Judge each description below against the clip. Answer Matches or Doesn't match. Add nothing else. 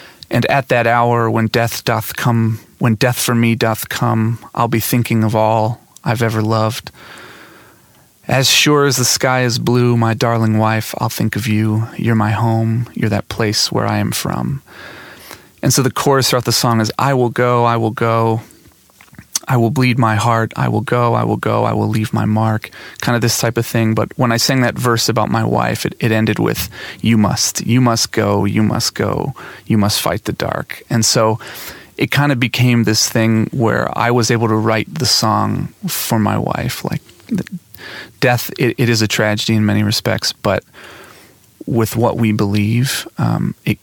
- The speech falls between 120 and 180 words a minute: Doesn't match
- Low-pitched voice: Matches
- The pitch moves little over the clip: Matches